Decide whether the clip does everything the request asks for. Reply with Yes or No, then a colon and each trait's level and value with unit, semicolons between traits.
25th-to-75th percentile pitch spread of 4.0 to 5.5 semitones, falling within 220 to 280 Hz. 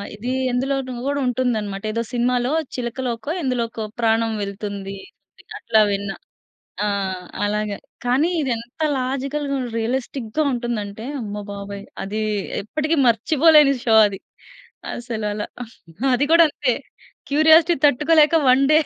Yes: average, 4.4 semitones; high, 245 Hz